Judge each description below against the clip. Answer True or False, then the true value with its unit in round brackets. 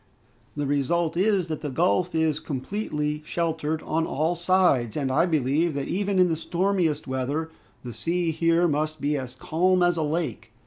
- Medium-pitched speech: True (160 Hz)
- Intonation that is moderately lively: True (3.1 semitones)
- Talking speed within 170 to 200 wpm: True (175 wpm)